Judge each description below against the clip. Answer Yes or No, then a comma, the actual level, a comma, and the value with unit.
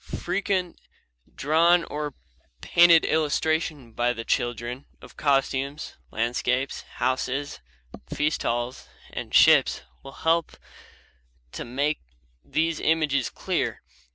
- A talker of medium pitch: Yes, medium, 145 Hz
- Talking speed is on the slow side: Yes, slow, 100 wpm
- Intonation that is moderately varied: Yes, average, 4.2 semitones